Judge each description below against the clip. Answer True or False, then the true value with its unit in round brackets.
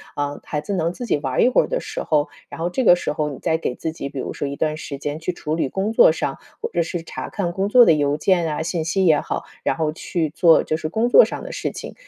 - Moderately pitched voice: True (160 Hz)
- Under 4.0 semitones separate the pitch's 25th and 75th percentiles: True (3.2 semitones)